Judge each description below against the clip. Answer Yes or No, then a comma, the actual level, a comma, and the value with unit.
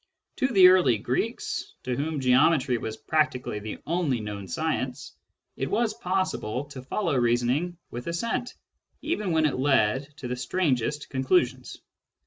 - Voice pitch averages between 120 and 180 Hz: Yes, low, 135 Hz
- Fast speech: No, average, 140 wpm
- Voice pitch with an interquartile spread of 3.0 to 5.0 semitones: No, wide, 5.4 semitones